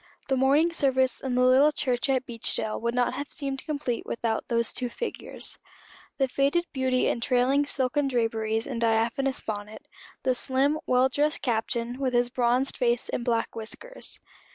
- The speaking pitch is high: Yes, very high, 255 Hz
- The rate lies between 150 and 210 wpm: Yes, average, 165 wpm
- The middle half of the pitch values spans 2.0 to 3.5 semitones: Yes, narrow, 2.6 semitones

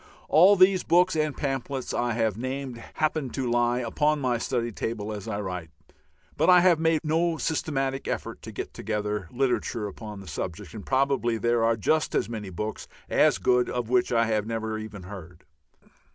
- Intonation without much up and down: No, average, 4.6 semitones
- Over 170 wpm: Yes, average, 180 wpm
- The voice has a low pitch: Yes, low, 120 Hz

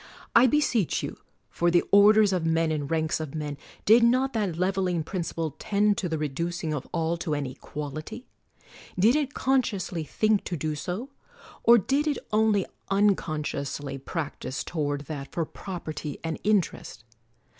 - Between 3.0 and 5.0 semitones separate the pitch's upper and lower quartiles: No, wide, 5.4 semitones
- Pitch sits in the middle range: Yes, medium, 175 Hz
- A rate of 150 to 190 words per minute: Yes, average, 160 wpm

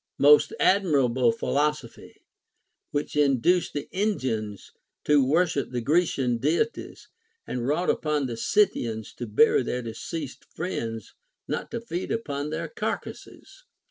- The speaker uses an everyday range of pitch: No, wide, 5.9 semitones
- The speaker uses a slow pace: Yes, slow, 120 wpm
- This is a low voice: No, medium, 145 Hz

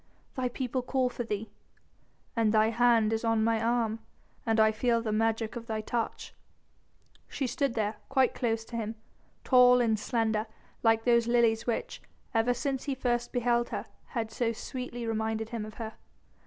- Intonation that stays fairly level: Yes, narrow, 1.7 semitones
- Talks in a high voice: Yes, high, 230 Hz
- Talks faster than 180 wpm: No, average, 170 wpm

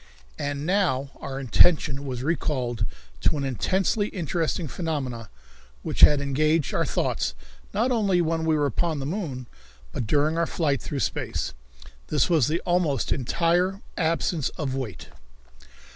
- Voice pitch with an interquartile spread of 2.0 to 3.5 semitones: No, average, 4.2 semitones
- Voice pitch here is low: No, medium, 150 Hz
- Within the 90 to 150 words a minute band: Yes, average, 145 wpm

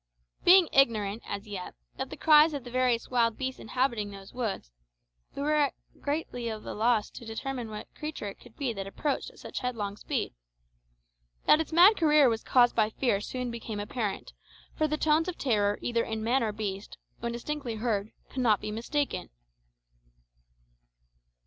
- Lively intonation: No, average, 4.6 semitones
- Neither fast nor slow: Yes, average, 170 wpm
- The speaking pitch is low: No, high, 235 Hz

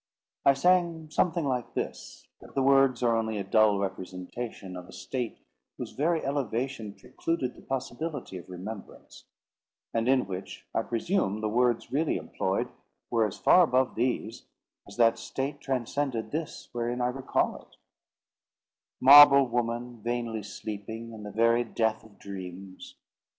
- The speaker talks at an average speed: Yes, average, 145 wpm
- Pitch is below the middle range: Yes, low, 120 Hz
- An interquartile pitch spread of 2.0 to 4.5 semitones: Yes, average, 3.9 semitones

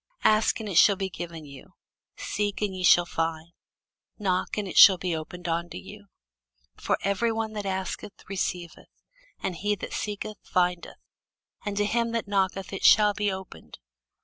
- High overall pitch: Yes, high, 195 Hz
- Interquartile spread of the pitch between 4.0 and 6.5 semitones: No, average, 2.8 semitones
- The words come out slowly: No, average, 170 wpm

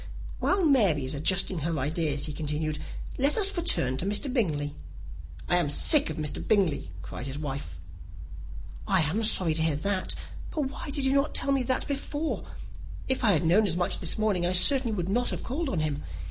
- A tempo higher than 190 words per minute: Yes, average, 200 wpm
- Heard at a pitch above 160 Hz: Yes, medium, 185 Hz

